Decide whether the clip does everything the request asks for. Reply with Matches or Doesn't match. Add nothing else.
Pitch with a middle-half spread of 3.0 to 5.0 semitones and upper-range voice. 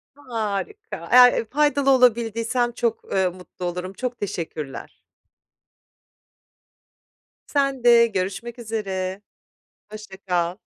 Matches